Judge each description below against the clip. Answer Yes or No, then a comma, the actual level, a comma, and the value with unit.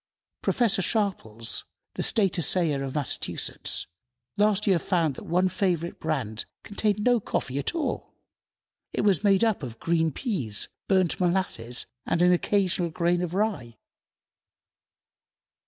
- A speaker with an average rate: No, slow, 130 wpm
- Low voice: No, medium, 180 Hz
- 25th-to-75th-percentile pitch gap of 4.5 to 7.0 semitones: Yes, average, 5.2 semitones